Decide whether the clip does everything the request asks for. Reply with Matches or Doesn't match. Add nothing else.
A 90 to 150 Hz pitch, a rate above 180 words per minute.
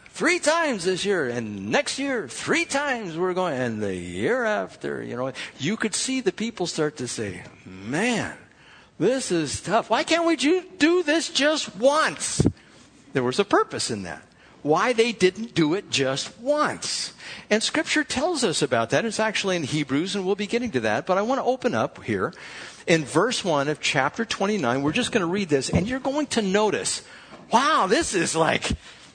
Doesn't match